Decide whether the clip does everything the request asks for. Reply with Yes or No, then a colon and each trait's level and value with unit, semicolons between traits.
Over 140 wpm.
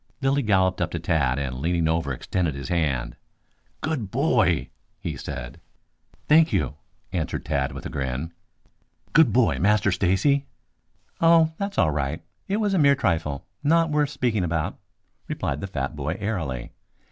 Yes: average, 155 wpm